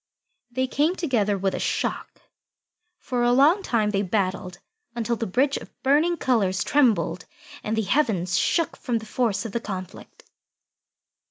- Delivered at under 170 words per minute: Yes, average, 155 wpm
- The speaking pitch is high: Yes, high, 230 Hz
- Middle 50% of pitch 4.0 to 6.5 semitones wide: Yes, average, 5.1 semitones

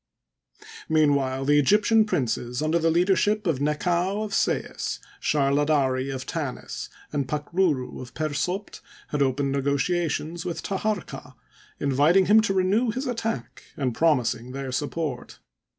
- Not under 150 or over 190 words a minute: No, slow, 135 wpm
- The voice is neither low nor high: Yes, medium, 155 Hz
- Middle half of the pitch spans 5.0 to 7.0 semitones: Yes, average, 5.3 semitones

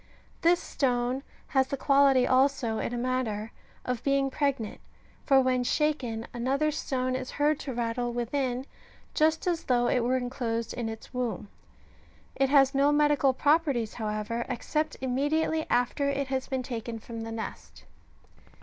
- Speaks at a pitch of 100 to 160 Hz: No, very high, 255 Hz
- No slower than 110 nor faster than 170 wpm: Yes, average, 150 wpm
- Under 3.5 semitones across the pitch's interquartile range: Yes, average, 2.8 semitones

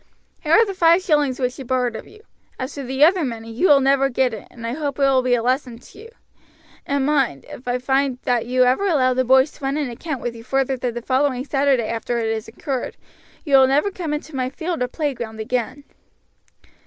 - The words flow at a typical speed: No, fast, 235 wpm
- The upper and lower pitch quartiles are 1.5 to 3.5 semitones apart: Yes, average, 2.8 semitones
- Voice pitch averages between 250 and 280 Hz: Yes, very high, 265 Hz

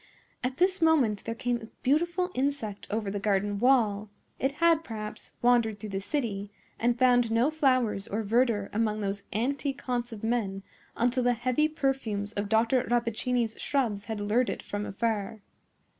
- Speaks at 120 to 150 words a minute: No, average, 165 wpm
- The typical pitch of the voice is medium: No, high, 230 Hz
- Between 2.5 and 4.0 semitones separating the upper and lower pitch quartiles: Yes, average, 3.6 semitones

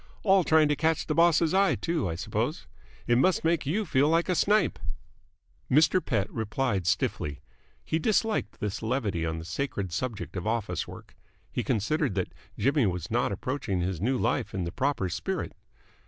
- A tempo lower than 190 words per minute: Yes, average, 175 wpm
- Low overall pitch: Yes, low, 130 Hz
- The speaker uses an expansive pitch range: Yes, wide, 8.6 semitones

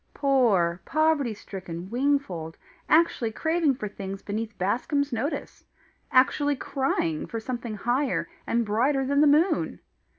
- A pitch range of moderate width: No, wide, 5.7 semitones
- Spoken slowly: Yes, slow, 125 wpm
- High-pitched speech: Yes, high, 245 Hz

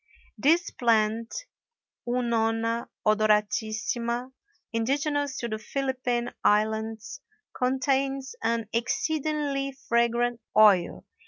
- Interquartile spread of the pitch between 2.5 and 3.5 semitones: Yes, average, 3.2 semitones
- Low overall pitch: No, high, 235 Hz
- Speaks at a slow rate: Yes, slow, 75 wpm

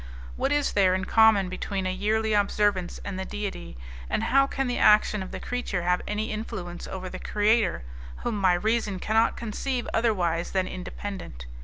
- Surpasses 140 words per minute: Yes, average, 175 wpm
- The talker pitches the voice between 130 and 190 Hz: No, high, 205 Hz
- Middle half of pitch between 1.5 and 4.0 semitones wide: Yes, average, 3.1 semitones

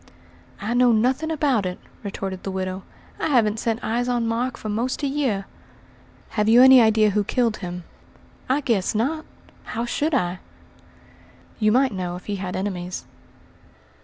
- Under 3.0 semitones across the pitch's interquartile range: No, average, 4.4 semitones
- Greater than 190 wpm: No, average, 160 wpm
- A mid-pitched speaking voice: No, high, 225 Hz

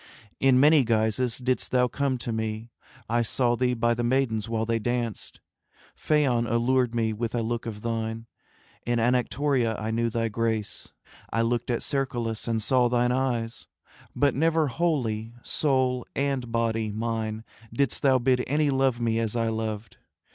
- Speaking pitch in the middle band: No, low, 120 Hz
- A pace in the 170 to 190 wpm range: No, average, 160 wpm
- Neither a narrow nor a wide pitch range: No, narrow, 2.2 semitones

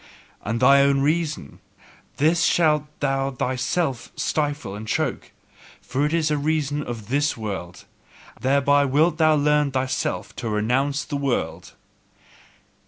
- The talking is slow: Yes, slow, 130 wpm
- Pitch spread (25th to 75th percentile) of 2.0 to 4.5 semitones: Yes, average, 2.8 semitones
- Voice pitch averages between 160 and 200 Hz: No, medium, 140 Hz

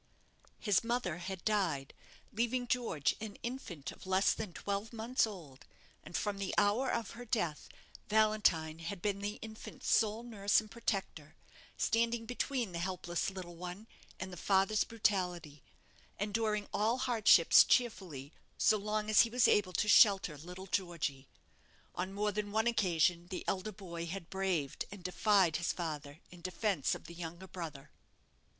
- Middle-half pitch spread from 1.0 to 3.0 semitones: No, average, 3.9 semitones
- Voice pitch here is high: Yes, high, 195 Hz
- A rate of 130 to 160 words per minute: Yes, average, 155 wpm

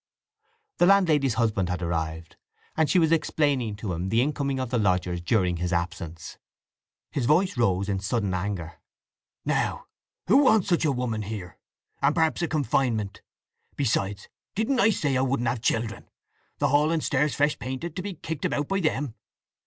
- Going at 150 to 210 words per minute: Yes, average, 170 wpm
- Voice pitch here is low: Yes, low, 125 Hz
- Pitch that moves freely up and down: Yes, wide, 7.6 semitones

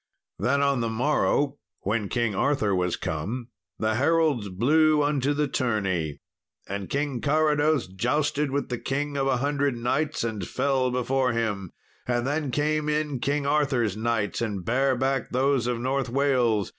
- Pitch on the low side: Yes, low, 130 Hz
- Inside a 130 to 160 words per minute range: Yes, average, 155 wpm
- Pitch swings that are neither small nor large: Yes, average, 3.9 semitones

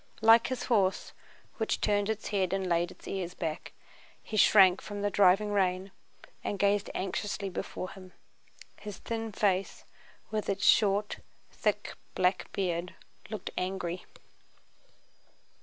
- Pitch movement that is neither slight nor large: No, narrow, 2.1 semitones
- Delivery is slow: Yes, slow, 130 wpm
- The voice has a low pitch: No, high, 195 Hz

